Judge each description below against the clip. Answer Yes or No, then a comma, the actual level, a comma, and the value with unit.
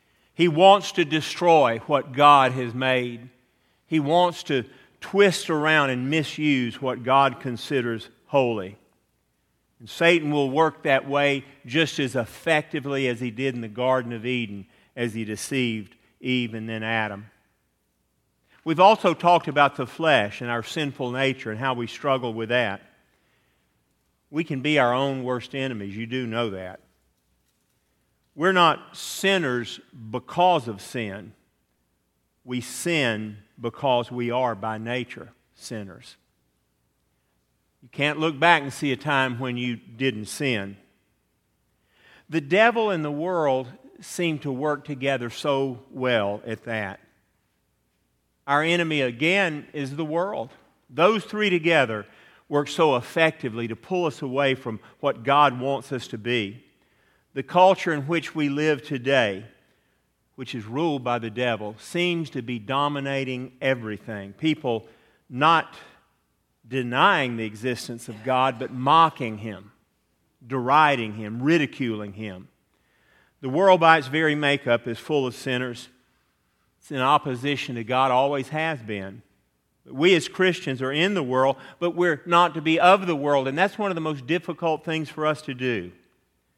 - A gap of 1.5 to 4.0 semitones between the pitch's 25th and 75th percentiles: No, average, 5.0 semitones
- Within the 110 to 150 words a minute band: Yes, average, 145 wpm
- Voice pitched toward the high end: No, low, 130 Hz